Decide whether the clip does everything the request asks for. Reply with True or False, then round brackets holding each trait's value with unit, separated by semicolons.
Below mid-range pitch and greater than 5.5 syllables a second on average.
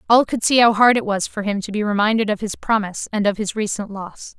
False (215 Hz; 6.0 syllables/s)